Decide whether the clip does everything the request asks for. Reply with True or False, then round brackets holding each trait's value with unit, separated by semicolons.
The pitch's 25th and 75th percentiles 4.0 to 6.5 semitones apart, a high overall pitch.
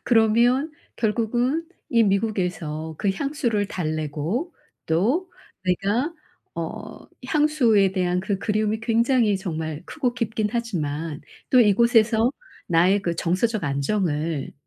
True (5.2 semitones; 210 Hz)